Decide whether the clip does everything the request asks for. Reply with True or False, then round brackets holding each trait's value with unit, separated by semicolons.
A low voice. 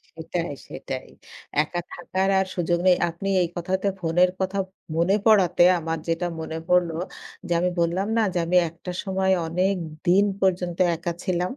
False (180 Hz)